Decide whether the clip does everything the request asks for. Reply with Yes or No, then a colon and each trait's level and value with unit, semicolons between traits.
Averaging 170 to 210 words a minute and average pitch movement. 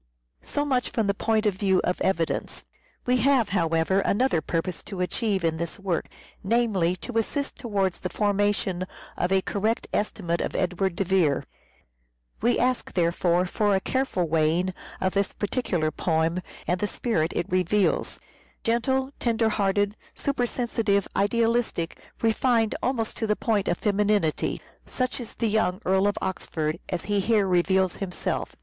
No: average, 155 wpm; average, 4.0 semitones